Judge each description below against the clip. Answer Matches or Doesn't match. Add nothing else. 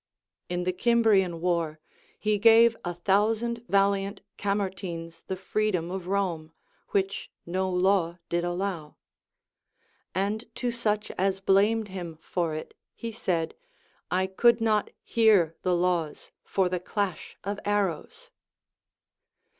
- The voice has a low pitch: Doesn't match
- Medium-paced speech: Doesn't match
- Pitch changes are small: Doesn't match